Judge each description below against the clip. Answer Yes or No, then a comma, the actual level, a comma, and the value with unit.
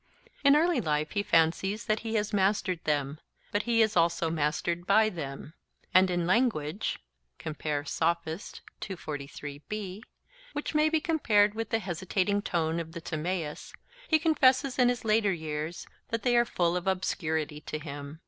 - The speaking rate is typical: Yes, average, 150 wpm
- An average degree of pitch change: No, wide, 5.7 semitones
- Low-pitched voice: No, medium, 185 Hz